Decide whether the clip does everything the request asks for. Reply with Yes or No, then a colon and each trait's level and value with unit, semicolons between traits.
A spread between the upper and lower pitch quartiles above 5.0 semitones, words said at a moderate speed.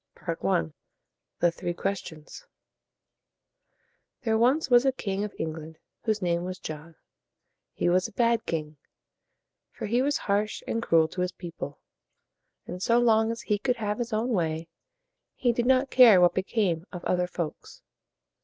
Yes: wide, 5.4 semitones; average, 155 wpm